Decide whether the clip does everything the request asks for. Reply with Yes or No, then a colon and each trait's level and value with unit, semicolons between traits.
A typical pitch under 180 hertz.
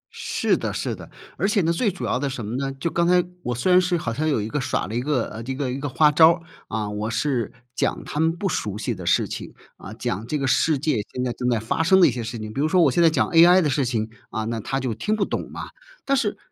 Yes: low, 135 Hz